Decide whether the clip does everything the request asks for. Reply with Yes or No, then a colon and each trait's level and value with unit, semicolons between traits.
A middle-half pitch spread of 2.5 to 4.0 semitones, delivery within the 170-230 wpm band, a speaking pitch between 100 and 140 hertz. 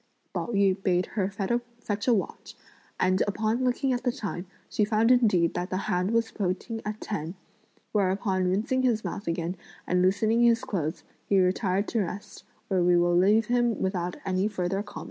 No: average, 3.5 semitones; average, 180 wpm; high, 200 Hz